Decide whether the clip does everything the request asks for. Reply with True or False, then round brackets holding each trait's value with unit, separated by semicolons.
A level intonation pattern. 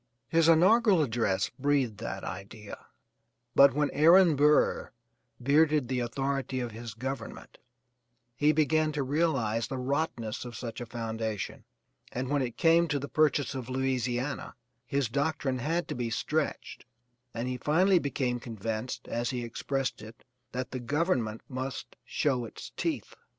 False (4.0 semitones)